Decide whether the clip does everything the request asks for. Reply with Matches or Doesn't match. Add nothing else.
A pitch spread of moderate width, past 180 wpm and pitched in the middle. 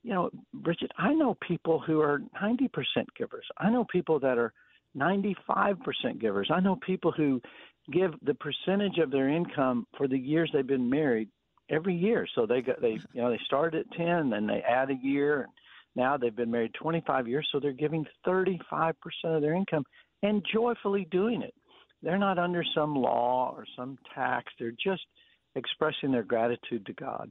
Doesn't match